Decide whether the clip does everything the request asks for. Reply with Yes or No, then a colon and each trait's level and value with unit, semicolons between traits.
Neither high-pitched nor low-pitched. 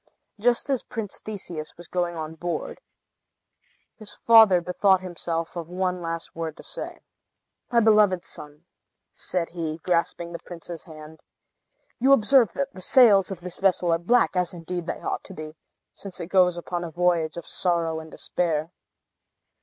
Yes: medium, 175 Hz